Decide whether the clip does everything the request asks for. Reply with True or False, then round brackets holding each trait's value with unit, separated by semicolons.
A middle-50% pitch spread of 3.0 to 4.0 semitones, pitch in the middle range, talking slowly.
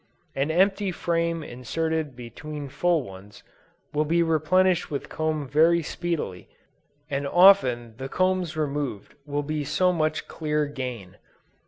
True (3.5 semitones; 155 Hz; 130 wpm)